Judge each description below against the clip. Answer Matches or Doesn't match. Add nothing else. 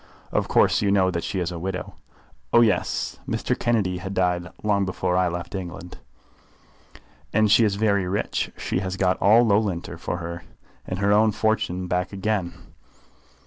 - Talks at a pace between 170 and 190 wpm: Matches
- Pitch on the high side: Doesn't match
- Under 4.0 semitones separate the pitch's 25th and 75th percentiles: Matches